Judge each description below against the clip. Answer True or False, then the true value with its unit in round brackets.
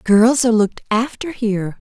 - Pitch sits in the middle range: False (230 Hz)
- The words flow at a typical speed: True (160 wpm)